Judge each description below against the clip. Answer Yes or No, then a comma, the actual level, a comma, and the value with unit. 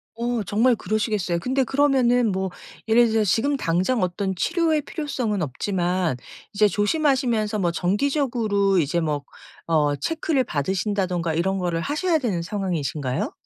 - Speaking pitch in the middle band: No, high, 205 Hz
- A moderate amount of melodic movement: No, wide, 6.2 semitones